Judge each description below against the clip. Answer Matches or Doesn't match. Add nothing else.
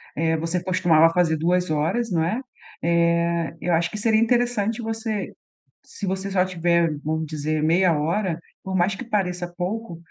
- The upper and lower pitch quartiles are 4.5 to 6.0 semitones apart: Doesn't match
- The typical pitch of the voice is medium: Matches